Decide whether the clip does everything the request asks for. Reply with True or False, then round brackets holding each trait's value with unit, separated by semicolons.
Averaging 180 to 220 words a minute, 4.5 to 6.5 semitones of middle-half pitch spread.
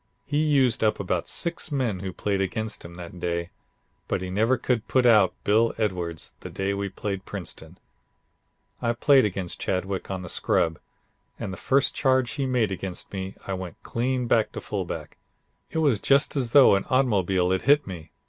True (185 wpm; 5.5 semitones)